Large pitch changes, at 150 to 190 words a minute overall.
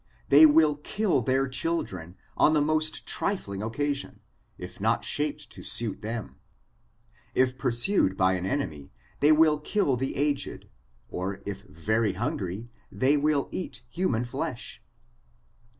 No: wide, 6.7 semitones; slow, 135 wpm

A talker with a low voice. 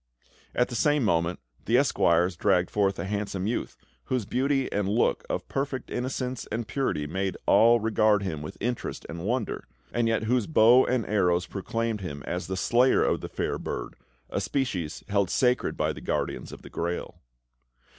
Yes: low, 110 Hz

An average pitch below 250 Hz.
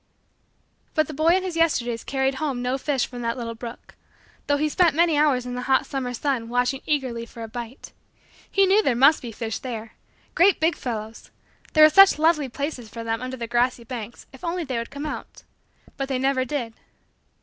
No: very high, 260 Hz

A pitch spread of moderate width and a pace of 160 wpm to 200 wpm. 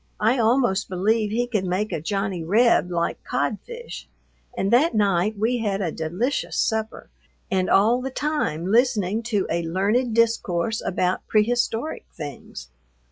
No: average, 4.4 semitones; average, 140 wpm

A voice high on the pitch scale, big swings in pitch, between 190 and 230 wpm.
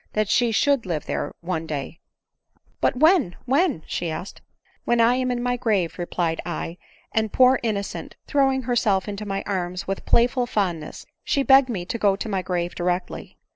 Yes: high, 205 Hz; wide, 5.7 semitones; average, 200 wpm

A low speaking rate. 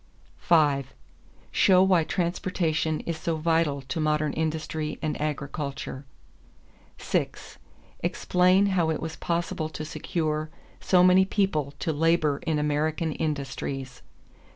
Yes: slow, 115 wpm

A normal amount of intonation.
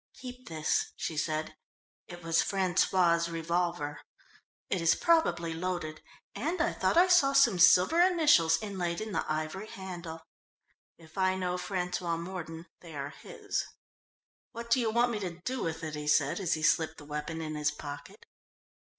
Yes: average, 3.8 semitones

